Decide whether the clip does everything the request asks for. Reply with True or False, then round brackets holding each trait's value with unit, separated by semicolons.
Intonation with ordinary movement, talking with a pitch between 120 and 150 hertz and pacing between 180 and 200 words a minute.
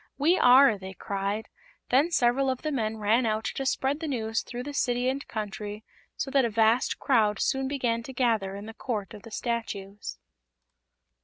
False (3.7 semitones; 235 Hz; 185 wpm)